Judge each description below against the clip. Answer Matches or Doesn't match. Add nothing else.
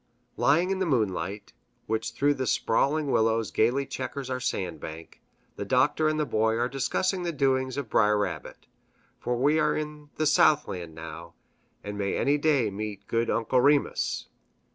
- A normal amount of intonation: Doesn't match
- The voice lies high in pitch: Doesn't match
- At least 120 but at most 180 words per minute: Matches